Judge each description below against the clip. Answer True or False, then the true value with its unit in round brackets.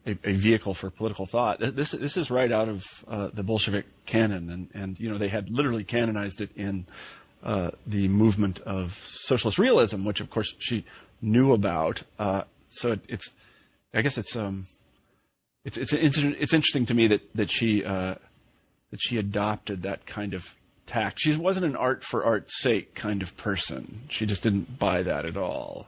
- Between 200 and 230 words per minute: False (190 wpm)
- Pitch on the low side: True (105 Hz)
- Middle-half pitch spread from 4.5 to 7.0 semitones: False (2.8 semitones)